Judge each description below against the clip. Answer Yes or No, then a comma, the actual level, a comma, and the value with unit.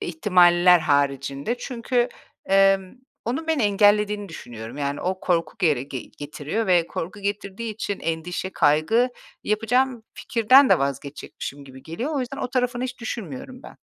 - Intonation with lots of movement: Yes, wide, 7.2 semitones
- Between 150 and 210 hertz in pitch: Yes, high, 195 Hz